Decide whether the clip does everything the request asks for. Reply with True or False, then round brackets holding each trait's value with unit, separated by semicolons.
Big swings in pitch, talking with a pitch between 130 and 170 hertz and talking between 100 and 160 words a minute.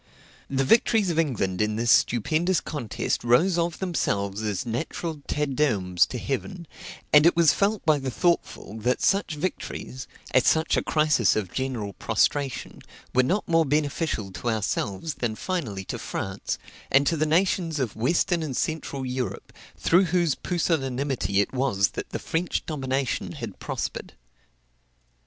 True (6.0 semitones; 140 Hz; 150 wpm)